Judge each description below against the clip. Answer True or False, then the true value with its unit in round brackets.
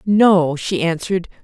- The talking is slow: True (125 wpm)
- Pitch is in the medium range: True (180 Hz)